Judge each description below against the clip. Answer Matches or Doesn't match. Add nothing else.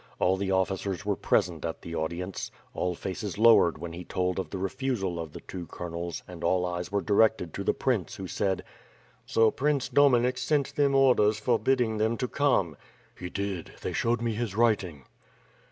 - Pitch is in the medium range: Doesn't match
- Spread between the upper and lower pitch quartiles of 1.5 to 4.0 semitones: Doesn't match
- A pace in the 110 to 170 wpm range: Doesn't match